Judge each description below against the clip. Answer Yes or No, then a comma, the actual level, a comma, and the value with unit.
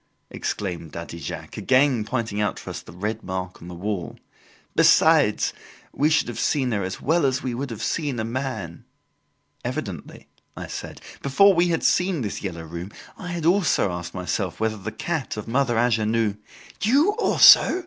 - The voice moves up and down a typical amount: No, wide, 6.7 semitones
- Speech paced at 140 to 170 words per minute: No, average, 180 wpm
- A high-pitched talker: No, low, 115 Hz